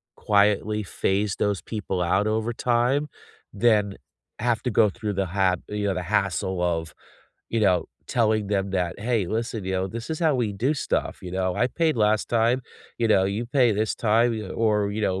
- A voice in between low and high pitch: No, low, 105 Hz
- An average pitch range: Yes, average, 3.2 semitones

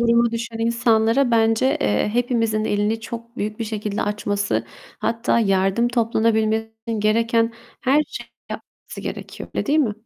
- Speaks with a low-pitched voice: No, high, 225 Hz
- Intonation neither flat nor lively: No, narrow, 1.6 semitones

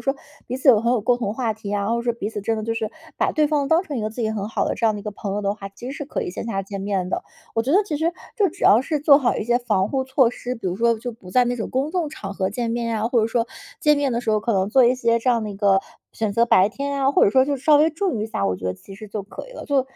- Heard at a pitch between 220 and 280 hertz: Yes, high, 230 Hz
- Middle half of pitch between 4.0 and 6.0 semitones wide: Yes, average, 4.5 semitones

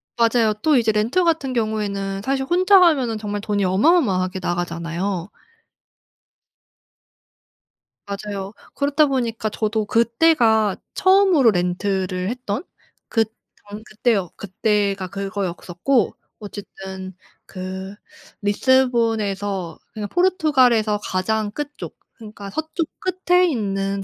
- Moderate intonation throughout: Yes, average, 4.9 semitones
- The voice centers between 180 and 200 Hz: No, high, 215 Hz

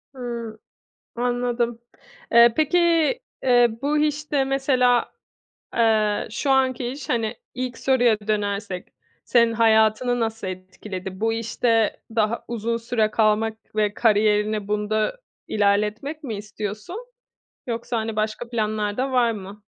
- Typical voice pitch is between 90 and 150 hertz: No, high, 225 Hz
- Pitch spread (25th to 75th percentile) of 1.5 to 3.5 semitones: Yes, narrow, 2.5 semitones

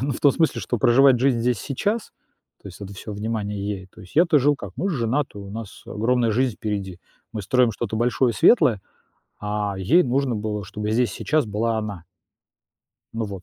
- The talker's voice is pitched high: No, low, 115 Hz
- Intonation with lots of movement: No, average, 4.0 semitones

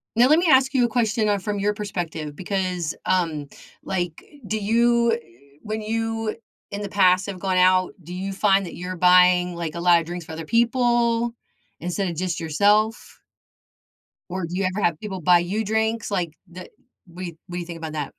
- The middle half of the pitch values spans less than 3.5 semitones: No, average, 3.8 semitones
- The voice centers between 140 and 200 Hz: Yes, medium, 185 Hz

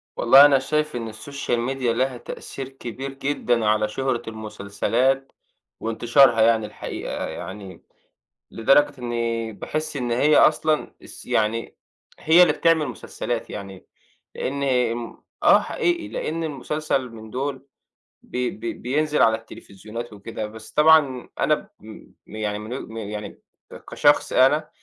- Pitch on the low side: Yes, low, 125 Hz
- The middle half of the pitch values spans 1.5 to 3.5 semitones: No, average, 4.1 semitones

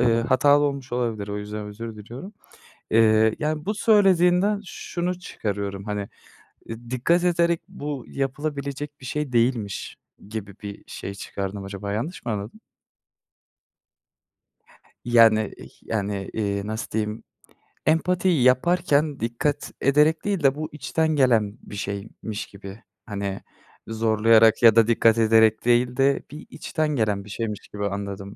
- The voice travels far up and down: Yes, wide, 5.8 semitones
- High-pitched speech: No, low, 115 Hz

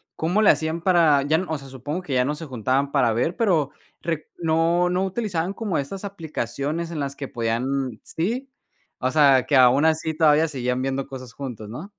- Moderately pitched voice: Yes, medium, 150 Hz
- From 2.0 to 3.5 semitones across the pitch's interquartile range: No, average, 4.3 semitones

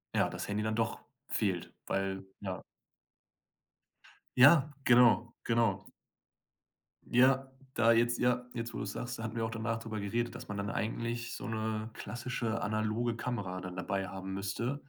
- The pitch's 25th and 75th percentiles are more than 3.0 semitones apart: No, narrow, 2.6 semitones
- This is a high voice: No, low, 115 Hz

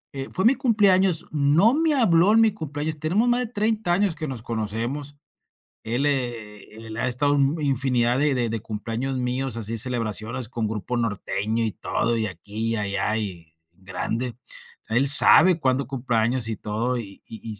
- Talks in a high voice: No, low, 125 Hz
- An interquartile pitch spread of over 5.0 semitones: Yes, wide, 5.5 semitones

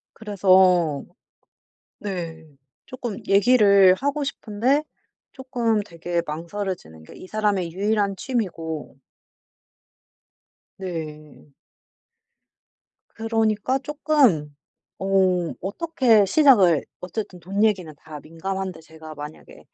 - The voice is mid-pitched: No, high, 195 Hz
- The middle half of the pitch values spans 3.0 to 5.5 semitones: Yes, average, 5.2 semitones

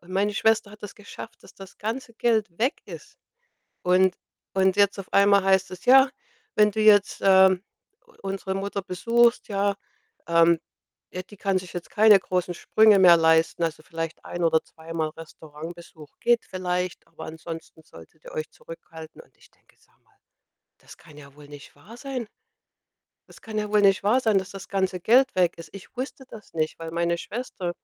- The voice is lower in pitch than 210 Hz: Yes, high, 190 Hz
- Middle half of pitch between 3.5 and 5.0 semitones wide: Yes, average, 4.0 semitones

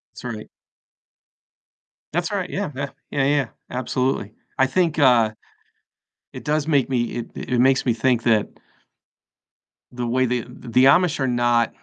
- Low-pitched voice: Yes, low, 130 Hz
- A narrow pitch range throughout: No, average, 3.0 semitones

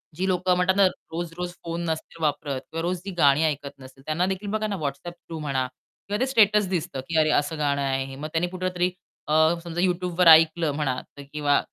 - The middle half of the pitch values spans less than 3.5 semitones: No, average, 3.8 semitones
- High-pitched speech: No, medium, 165 Hz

